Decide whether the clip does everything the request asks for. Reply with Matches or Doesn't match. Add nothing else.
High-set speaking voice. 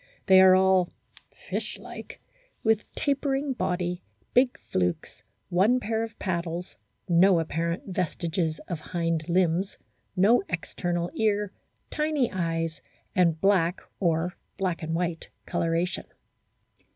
Doesn't match